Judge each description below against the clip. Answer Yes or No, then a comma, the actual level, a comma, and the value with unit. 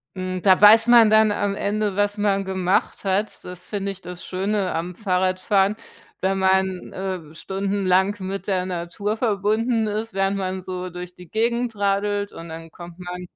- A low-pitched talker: No, high, 195 Hz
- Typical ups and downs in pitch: No, narrow, 2.1 semitones